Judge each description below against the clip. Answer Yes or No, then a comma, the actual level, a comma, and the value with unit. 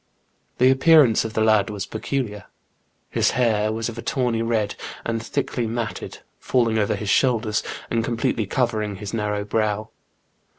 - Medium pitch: No, low, 110 Hz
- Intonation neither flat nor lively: No, narrow, 1.9 semitones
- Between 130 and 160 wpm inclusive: Yes, average, 155 wpm